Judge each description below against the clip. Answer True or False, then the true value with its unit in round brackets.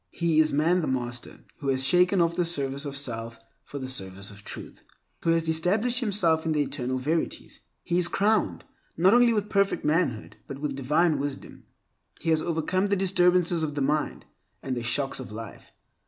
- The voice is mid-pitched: True (155 Hz)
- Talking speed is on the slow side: False (190 wpm)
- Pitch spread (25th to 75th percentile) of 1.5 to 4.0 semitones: False (4.9 semitones)